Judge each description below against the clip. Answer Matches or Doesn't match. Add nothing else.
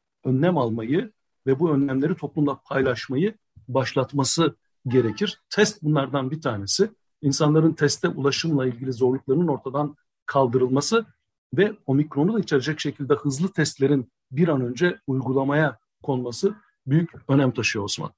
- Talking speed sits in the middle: Matches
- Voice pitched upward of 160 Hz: Doesn't match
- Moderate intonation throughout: Matches